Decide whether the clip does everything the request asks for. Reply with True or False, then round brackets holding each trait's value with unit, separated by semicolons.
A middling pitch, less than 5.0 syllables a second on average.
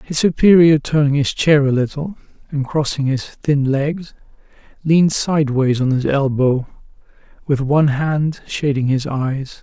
True (145 Hz; 4.4 syllables/s)